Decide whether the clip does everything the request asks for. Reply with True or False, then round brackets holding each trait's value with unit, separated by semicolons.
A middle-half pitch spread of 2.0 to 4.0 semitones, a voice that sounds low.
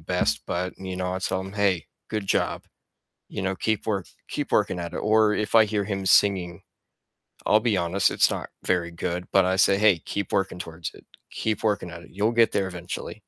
True (2.6 semitones; 95 Hz)